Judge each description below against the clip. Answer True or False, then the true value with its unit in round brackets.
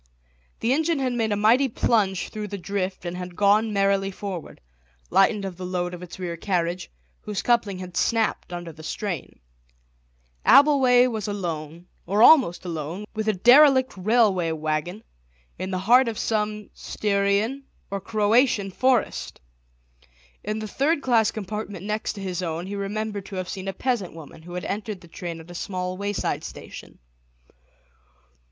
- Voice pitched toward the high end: True (200 Hz)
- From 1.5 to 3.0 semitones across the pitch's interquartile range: False (3.4 semitones)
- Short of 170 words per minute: True (160 wpm)